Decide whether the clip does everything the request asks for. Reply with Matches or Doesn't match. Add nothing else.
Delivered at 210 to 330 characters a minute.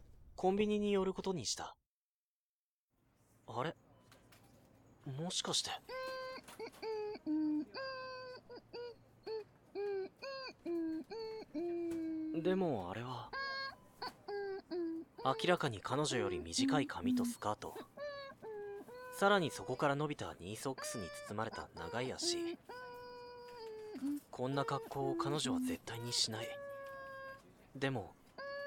Doesn't match